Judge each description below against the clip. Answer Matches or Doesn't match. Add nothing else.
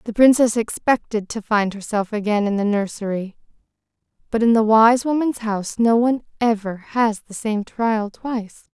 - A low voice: Doesn't match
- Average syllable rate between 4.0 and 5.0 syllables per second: Matches